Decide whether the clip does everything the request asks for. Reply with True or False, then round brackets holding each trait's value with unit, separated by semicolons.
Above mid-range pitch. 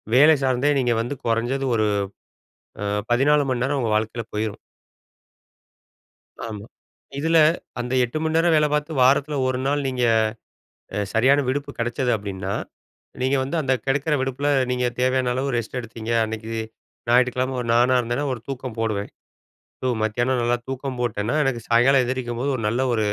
False (125 Hz)